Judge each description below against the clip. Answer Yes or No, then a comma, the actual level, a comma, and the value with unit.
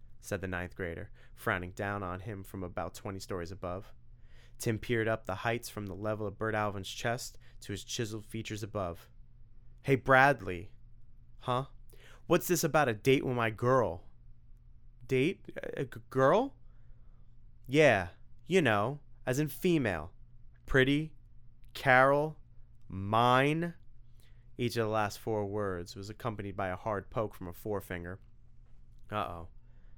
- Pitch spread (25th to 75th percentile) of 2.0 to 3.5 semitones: No, average, 4.0 semitones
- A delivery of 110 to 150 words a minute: Yes, average, 140 wpm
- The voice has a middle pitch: No, low, 115 Hz